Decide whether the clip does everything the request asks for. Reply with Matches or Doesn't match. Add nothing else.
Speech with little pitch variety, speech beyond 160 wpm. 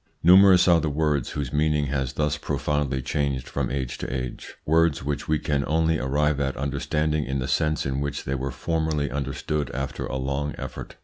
Matches